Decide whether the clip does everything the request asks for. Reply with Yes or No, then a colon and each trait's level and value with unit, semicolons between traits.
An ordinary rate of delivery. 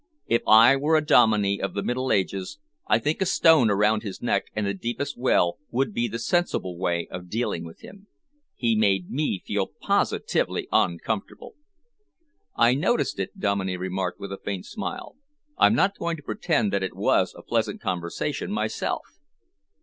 Yes: average, 170 wpm